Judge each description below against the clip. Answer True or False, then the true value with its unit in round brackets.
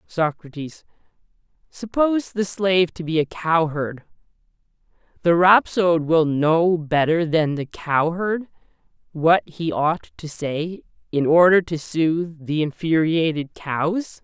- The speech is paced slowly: True (120 wpm)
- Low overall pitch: False (165 Hz)